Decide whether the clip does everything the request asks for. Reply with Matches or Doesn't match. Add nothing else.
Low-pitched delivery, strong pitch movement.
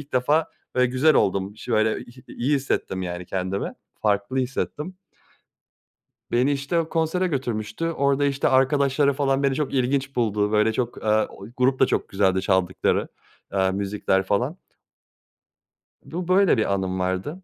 Matches